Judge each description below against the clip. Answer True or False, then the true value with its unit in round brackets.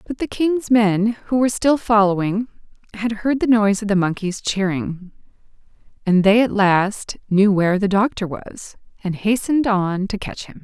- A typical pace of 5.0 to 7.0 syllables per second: False (4.7 syllables/s)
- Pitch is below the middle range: False (210 Hz)